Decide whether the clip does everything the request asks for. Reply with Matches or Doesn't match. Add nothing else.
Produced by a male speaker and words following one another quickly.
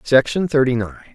Doesn't match